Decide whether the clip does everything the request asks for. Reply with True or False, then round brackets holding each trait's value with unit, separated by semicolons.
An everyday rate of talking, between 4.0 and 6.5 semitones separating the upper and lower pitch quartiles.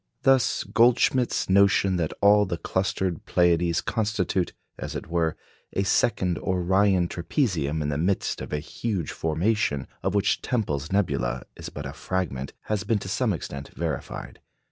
True (150 wpm; 4.3 semitones)